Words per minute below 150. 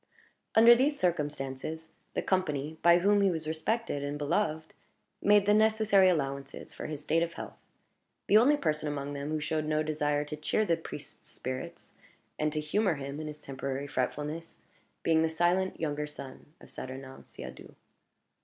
No: average, 165 wpm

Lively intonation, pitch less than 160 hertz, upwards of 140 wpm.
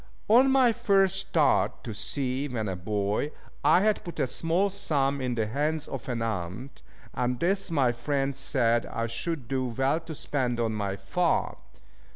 Yes: wide, 6.2 semitones; low, 135 Hz; average, 175 wpm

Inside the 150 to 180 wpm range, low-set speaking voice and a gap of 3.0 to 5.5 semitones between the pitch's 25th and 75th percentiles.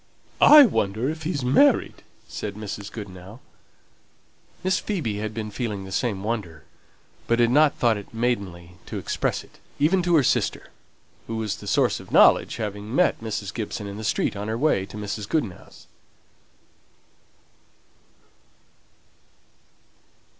No: average, 140 wpm; low, 110 Hz; average, 4.1 semitones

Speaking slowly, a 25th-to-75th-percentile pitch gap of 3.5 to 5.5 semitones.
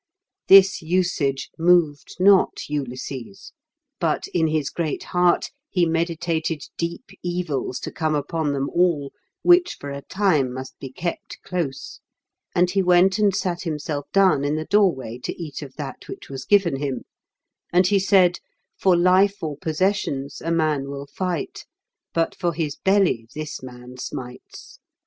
No: average, 155 wpm; average, 4.4 semitones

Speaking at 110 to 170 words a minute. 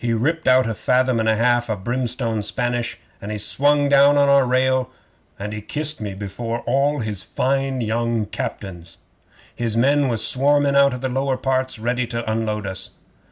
No: average, 185 wpm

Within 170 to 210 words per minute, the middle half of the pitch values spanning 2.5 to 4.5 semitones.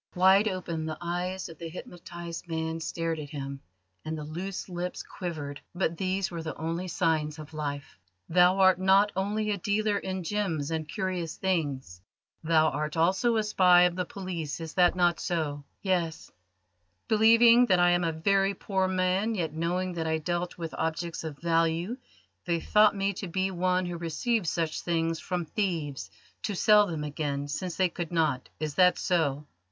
Yes: average, 180 wpm; average, 2.8 semitones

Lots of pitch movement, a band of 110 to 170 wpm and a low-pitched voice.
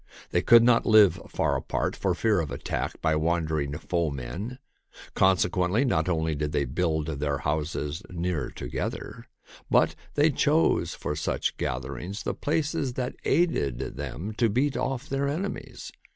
Yes: wide, 8.0 semitones; average, 150 wpm; very low, 90 Hz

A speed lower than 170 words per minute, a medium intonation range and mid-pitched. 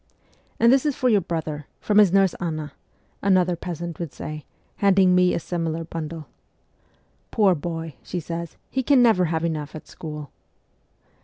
No: average, 175 wpm; average, 3.4 semitones; medium, 170 Hz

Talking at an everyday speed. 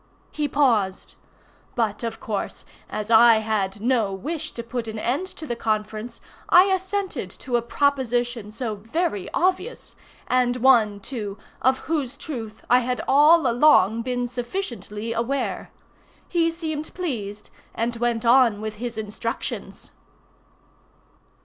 No: slow, 130 wpm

